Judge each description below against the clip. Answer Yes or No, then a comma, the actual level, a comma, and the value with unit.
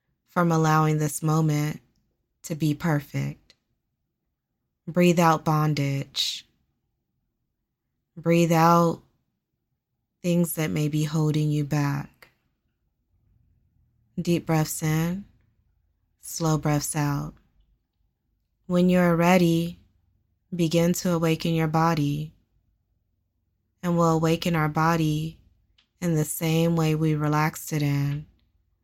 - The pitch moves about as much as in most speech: Yes, average, 4.5 semitones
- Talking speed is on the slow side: Yes, slow, 100 wpm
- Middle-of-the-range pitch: Yes, medium, 155 Hz